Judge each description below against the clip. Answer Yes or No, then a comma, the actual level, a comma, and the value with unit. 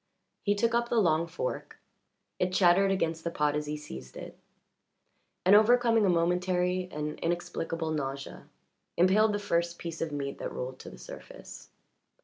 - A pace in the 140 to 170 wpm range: Yes, average, 160 wpm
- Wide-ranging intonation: No, average, 4.7 semitones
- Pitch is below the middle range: No, medium, 175 Hz